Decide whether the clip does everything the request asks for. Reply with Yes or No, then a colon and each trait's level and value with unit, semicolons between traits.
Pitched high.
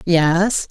No: medium, 180 Hz